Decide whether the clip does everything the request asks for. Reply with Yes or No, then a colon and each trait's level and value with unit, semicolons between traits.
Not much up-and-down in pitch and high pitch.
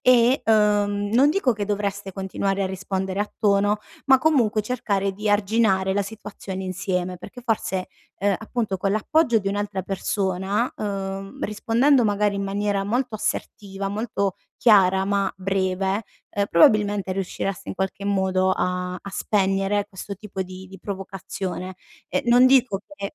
Yes: narrow, 1.8 semitones; high, 200 Hz